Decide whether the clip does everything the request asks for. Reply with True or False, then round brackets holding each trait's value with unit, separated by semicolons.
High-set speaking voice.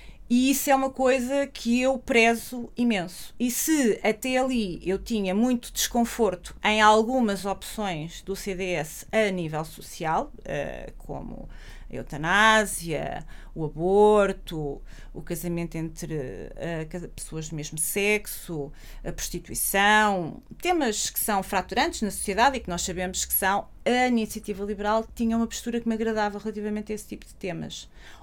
True (210 Hz)